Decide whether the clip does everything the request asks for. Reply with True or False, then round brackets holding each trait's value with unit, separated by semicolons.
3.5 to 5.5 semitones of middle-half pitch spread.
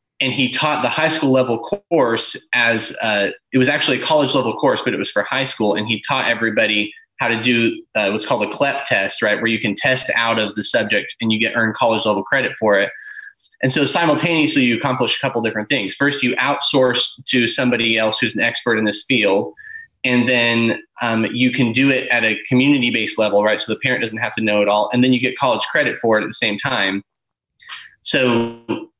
False (3.0 semitones)